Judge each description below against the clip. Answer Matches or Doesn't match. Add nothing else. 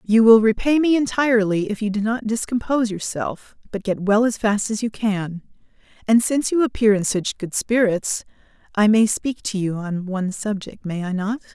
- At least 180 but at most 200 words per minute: Matches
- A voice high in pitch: Matches